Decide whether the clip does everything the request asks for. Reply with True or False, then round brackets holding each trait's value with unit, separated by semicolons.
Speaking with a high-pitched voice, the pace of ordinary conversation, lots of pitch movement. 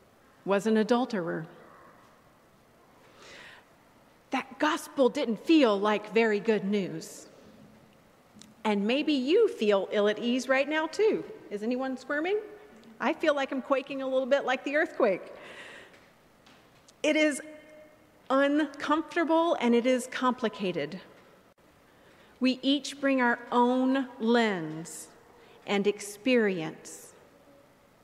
False (260 Hz; 105 wpm; 5.8 semitones)